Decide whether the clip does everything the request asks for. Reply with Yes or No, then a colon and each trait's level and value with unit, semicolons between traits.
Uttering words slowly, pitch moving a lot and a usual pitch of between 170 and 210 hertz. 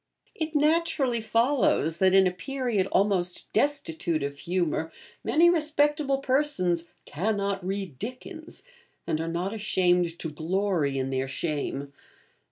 Yes: slow, 125 wpm; wide, 8.4 semitones; high, 190 Hz